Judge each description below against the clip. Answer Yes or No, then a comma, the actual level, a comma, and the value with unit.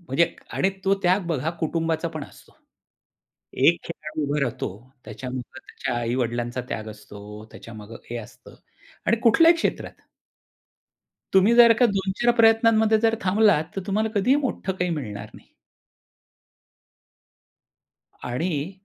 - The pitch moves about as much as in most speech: No, wide, 9.0 semitones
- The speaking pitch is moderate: Yes, medium, 165 Hz